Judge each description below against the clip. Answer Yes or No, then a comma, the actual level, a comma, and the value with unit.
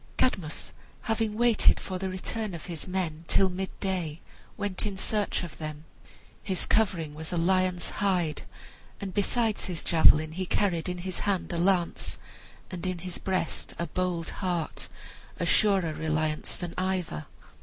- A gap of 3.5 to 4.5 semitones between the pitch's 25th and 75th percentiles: No, narrow, 2.6 semitones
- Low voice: No, medium, 185 Hz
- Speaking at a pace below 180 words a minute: Yes, average, 155 wpm